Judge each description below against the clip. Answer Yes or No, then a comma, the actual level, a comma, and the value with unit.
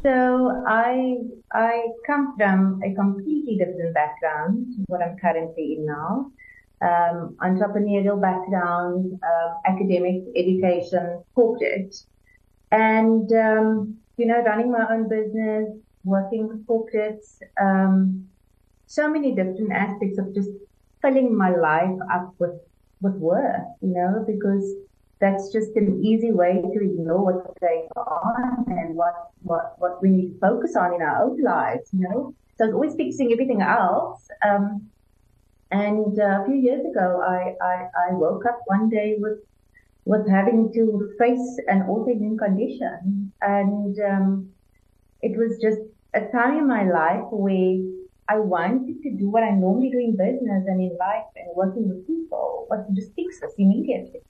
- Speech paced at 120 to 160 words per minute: Yes, average, 150 wpm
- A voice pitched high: Yes, high, 200 Hz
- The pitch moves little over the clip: No, average, 3.7 semitones